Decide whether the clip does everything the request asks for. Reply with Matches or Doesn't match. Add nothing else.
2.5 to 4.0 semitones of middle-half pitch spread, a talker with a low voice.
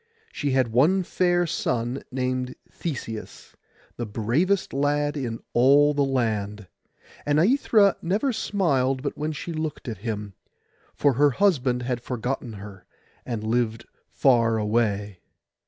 Doesn't match